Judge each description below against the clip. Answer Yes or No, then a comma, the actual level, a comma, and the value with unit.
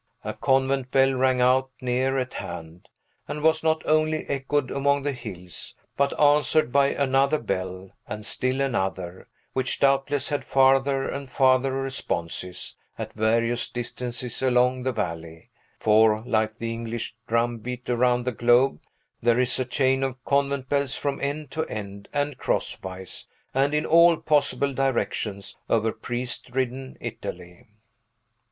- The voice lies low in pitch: Yes, low, 130 Hz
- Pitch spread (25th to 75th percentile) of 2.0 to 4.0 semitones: Yes, average, 3.2 semitones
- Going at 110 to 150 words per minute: Yes, average, 140 wpm